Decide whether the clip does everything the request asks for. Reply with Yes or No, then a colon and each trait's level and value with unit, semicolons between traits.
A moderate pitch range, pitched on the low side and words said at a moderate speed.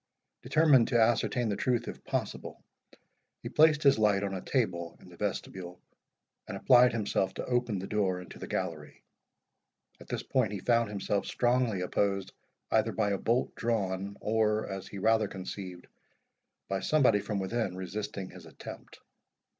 Yes: average, 3.7 semitones; low, 105 Hz; average, 160 wpm